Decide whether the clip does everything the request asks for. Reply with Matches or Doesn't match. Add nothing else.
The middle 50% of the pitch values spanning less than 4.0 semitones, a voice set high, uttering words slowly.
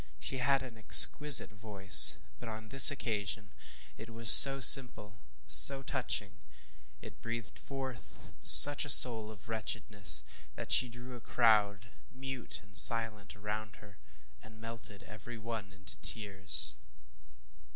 Doesn't match